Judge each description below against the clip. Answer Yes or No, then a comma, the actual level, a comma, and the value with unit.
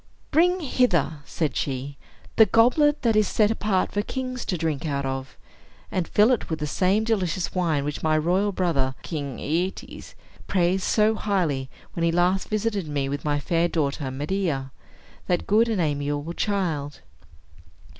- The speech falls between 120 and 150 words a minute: No, average, 160 wpm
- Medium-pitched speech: Yes, medium, 175 Hz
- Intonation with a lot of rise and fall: Yes, wide, 6.2 semitones